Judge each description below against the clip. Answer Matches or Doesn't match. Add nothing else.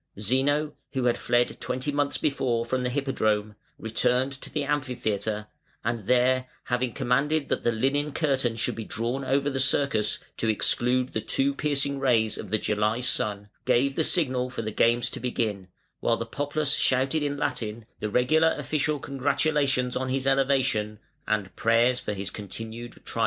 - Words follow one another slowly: Doesn't match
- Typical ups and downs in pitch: Matches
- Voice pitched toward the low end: Matches